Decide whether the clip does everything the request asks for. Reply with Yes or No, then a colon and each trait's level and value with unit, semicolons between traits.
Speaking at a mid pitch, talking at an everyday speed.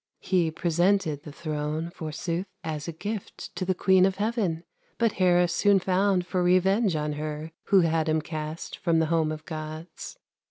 Yes: medium, 170 Hz; average, 170 wpm